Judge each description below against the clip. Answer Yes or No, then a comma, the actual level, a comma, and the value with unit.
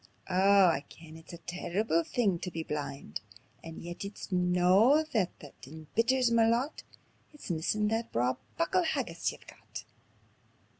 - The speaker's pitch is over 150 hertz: Yes, medium, 185 Hz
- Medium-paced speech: Yes, average, 150 wpm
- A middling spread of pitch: No, wide, 5.8 semitones